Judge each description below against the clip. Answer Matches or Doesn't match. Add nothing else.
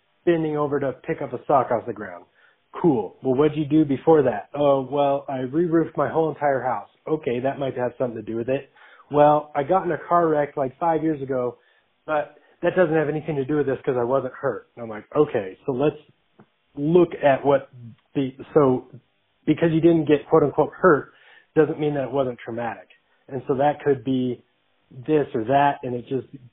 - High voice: Doesn't match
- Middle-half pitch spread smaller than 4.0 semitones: Matches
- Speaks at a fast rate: Matches